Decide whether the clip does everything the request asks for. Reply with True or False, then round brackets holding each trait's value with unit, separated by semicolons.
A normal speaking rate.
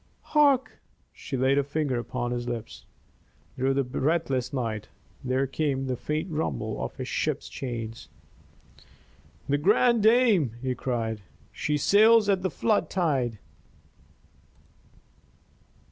False (120 wpm)